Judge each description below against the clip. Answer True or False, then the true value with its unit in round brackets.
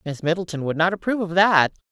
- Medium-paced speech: False (220 wpm)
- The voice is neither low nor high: True (175 Hz)